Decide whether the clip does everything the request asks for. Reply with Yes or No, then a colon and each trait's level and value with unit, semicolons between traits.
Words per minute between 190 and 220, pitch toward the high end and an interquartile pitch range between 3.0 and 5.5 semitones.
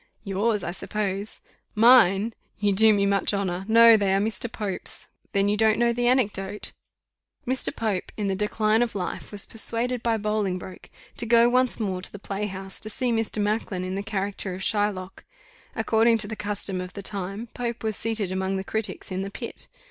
No: average, 195 wpm; high, 210 Hz; narrow, 2.6 semitones